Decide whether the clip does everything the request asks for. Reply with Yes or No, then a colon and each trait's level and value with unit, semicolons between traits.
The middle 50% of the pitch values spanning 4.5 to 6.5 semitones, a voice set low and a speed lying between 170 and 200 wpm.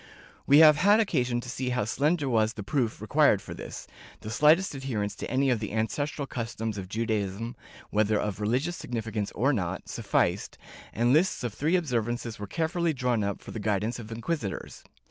Yes: average, 4.9 semitones; low, 120 Hz; average, 190 wpm